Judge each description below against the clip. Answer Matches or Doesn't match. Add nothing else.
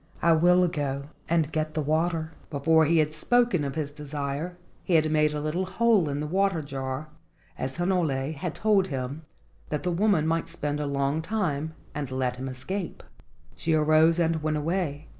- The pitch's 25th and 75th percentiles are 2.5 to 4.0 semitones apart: Matches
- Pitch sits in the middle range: Matches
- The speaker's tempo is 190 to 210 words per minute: Doesn't match